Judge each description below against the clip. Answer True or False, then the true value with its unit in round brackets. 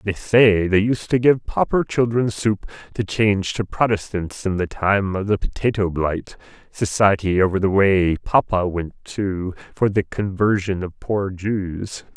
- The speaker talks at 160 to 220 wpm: True (165 wpm)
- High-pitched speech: False (100 Hz)